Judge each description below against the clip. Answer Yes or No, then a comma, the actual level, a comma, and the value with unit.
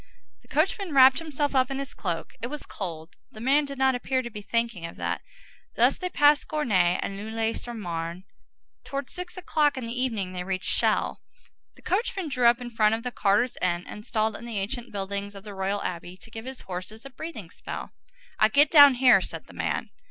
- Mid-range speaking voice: No, high, 235 Hz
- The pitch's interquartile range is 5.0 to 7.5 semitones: Yes, wide, 5.6 semitones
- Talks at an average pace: No, fast, 210 wpm